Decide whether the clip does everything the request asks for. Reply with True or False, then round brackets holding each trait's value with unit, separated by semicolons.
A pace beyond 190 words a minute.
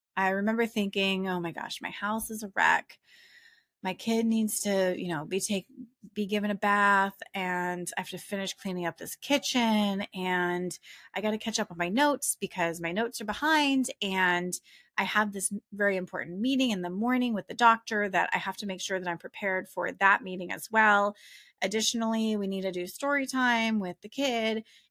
True (200 wpm)